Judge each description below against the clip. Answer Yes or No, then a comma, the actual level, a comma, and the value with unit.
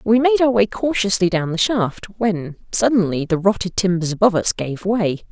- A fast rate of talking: No, average, 190 wpm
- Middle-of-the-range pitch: No, high, 200 Hz